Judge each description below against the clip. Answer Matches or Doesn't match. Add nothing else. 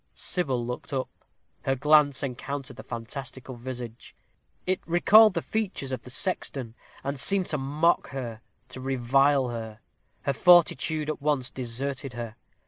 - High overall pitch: Doesn't match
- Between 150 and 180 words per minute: Doesn't match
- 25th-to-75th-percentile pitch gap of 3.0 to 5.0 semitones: Matches